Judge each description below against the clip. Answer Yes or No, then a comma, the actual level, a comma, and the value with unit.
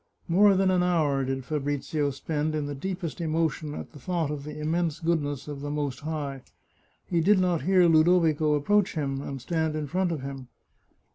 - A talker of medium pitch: Yes, medium, 155 Hz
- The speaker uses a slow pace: No, average, 190 wpm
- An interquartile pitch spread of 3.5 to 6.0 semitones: No, average, 3.1 semitones